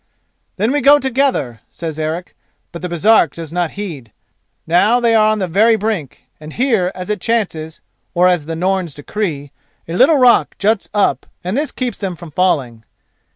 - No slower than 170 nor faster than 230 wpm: Yes, average, 180 wpm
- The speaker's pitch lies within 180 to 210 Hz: Yes, medium, 185 Hz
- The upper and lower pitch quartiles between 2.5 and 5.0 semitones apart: No, wide, 5.5 semitones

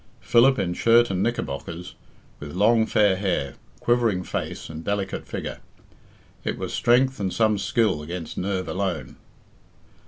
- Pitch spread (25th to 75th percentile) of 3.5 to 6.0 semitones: Yes, average, 4.6 semitones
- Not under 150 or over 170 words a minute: No, slow, 135 wpm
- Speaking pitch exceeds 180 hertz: No, low, 100 Hz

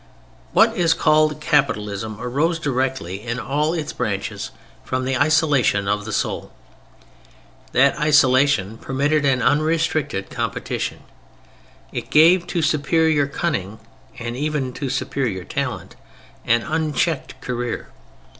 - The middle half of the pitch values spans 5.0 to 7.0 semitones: No, average, 4.2 semitones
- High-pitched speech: No, medium, 140 Hz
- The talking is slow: Yes, slow, 115 wpm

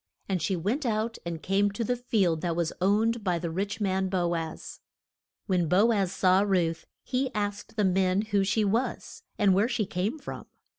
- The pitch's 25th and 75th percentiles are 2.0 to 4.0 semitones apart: Yes, average, 3.1 semitones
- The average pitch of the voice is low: No, high, 195 Hz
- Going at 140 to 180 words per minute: No, average, 195 wpm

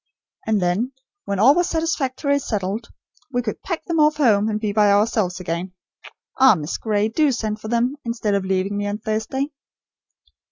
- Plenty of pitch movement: No, average, 4.7 semitones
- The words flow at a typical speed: Yes, average, 175 wpm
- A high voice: Yes, high, 220 Hz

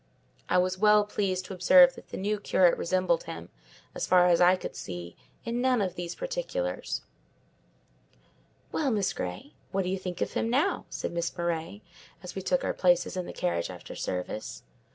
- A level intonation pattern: No, average, 3.5 semitones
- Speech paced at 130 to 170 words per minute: No, average, 185 wpm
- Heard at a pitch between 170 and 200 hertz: Yes, medium, 185 Hz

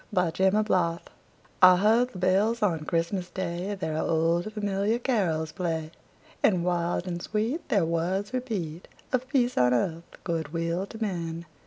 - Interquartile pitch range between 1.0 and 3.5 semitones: No, average, 4.0 semitones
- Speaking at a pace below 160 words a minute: Yes, average, 150 wpm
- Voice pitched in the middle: Yes, medium, 180 Hz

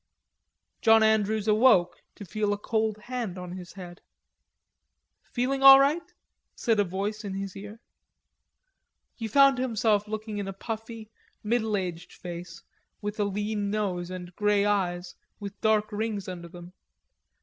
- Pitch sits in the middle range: No, high, 210 Hz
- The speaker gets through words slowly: No, average, 145 wpm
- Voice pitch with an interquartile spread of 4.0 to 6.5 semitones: No, average, 2.8 semitones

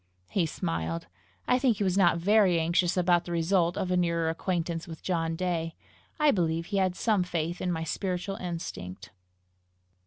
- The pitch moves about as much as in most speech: No, narrow, 2.2 semitones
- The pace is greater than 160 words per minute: Yes, average, 175 wpm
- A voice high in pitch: No, medium, 175 Hz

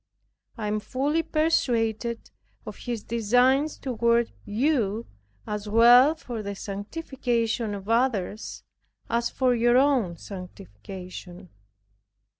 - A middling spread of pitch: Yes, average, 3.7 semitones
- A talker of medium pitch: No, high, 230 Hz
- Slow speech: Yes, slow, 100 wpm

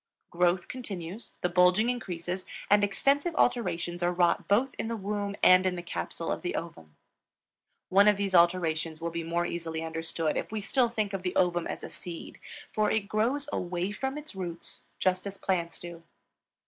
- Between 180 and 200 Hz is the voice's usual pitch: Yes, medium, 185 Hz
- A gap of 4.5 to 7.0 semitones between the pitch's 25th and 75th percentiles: No, average, 3.5 semitones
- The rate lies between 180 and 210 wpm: Yes, average, 185 wpm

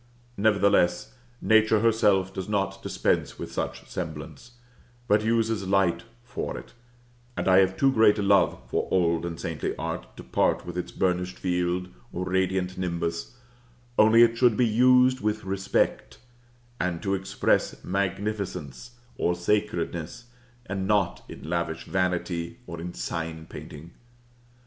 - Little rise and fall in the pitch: No, average, 3.4 semitones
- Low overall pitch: Yes, very low, 95 Hz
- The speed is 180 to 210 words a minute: No, average, 140 wpm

